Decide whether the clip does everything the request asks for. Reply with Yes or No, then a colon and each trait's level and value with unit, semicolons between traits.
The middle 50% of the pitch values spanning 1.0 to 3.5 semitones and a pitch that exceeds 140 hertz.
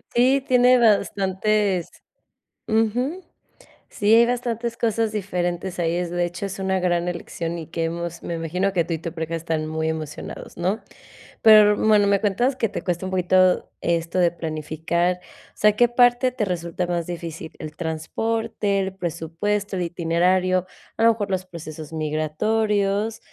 No: average, 4.2 semitones; medium, 185 Hz